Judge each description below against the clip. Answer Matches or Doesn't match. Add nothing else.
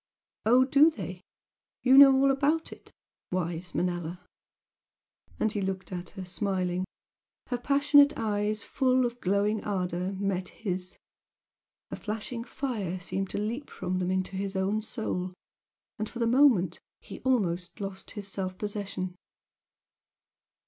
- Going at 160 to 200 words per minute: Doesn't match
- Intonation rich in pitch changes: Doesn't match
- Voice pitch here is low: Doesn't match